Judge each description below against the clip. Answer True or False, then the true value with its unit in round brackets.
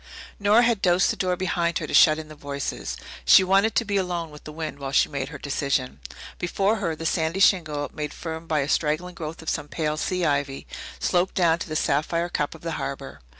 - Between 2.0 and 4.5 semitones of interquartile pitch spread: True (3.4 semitones)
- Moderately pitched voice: True (160 Hz)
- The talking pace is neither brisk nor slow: False (225 wpm)